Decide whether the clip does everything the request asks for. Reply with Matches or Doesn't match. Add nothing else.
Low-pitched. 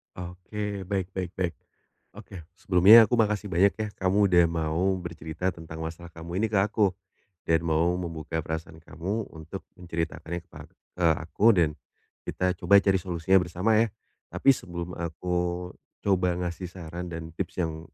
Matches